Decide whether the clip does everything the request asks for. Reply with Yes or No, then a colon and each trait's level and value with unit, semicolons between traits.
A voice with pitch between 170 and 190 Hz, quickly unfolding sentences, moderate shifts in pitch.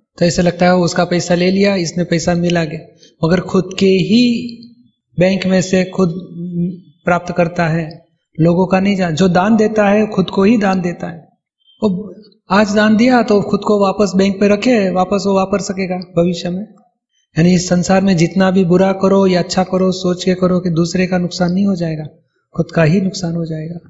No: medium, 185 Hz; fast, 205 wpm; narrow, 2.2 semitones